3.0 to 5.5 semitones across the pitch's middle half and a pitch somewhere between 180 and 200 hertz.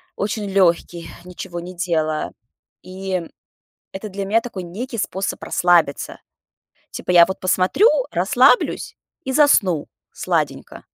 No: narrow, 2.6 semitones; medium, 185 Hz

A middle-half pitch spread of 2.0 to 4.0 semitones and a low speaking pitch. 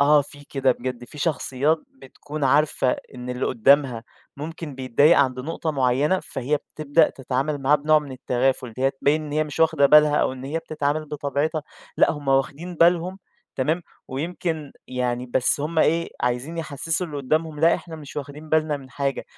No: average, 2.8 semitones; medium, 145 Hz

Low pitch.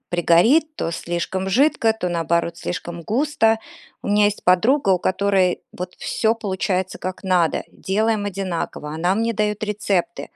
No: high, 190 Hz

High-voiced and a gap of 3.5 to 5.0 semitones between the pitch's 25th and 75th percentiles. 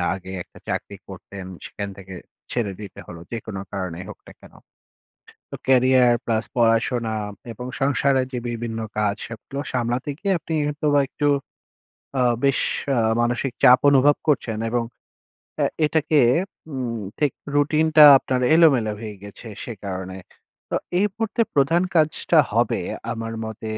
No: low, 120 Hz; average, 4.5 semitones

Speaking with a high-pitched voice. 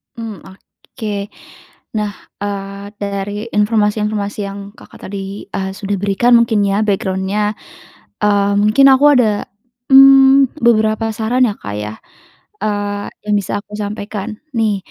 Yes: high, 205 Hz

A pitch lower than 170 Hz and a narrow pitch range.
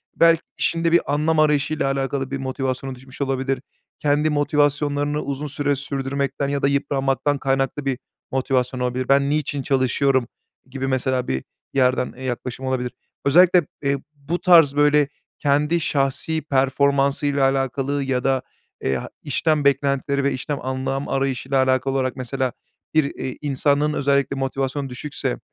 Yes: medium, 140 Hz; narrow, 1.6 semitones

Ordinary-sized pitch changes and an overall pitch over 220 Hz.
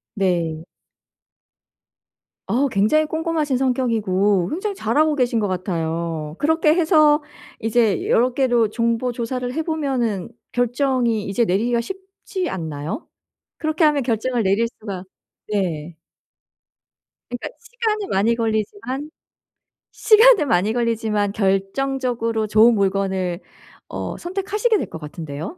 No: wide, 7.1 semitones; high, 235 Hz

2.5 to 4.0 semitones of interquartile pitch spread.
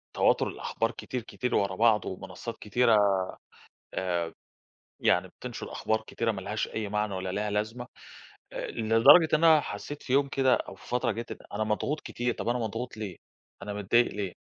Yes: average, 3.1 semitones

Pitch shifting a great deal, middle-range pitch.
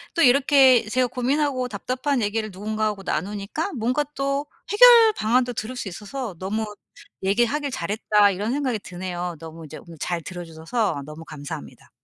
No: wide, 5.8 semitones; high, 220 Hz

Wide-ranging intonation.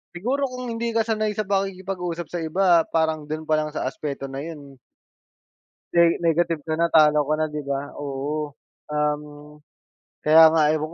No: average, 3.6 semitones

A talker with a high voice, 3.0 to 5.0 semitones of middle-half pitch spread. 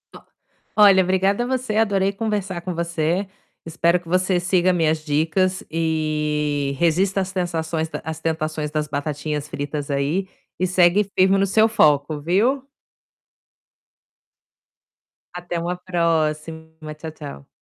No: medium, 170 Hz; average, 3.5 semitones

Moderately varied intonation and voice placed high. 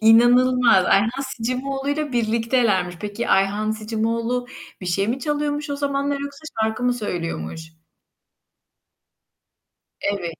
Yes: average, 4.7 semitones; high, 230 Hz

